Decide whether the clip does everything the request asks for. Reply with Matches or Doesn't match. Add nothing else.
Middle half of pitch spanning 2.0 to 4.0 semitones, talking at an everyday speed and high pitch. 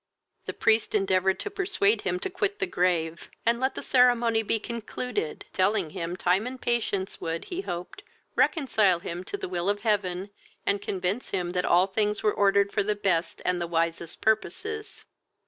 Doesn't match